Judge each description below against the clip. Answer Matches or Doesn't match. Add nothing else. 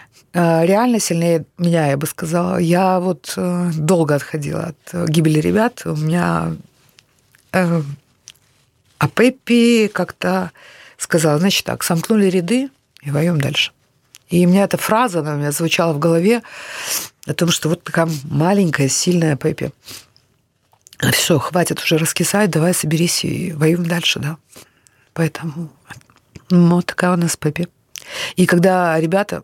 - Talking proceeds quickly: Doesn't match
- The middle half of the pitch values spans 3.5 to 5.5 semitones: Doesn't match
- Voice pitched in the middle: Matches